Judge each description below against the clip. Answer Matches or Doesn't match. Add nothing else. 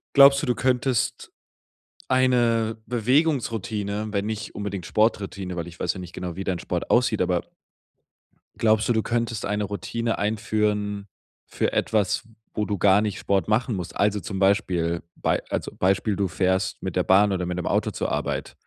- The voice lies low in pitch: Matches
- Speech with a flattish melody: Doesn't match